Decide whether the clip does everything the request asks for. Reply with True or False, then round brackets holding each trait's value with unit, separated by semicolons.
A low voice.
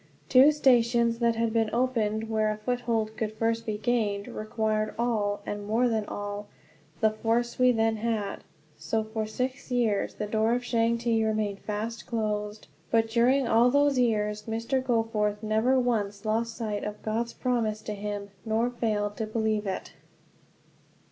False (225 Hz)